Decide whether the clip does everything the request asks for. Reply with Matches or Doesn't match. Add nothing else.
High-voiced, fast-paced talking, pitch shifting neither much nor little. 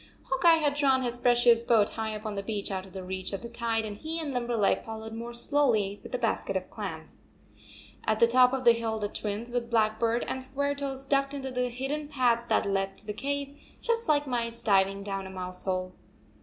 Matches